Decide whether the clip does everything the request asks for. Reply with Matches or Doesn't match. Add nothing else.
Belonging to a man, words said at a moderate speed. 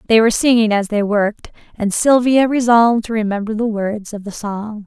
Doesn't match